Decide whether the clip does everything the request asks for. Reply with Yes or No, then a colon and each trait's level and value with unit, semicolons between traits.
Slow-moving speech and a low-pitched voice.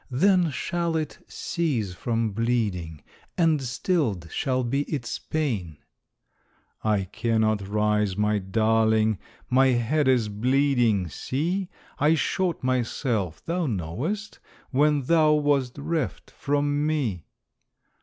Yes: slow, 110 wpm; low, 125 Hz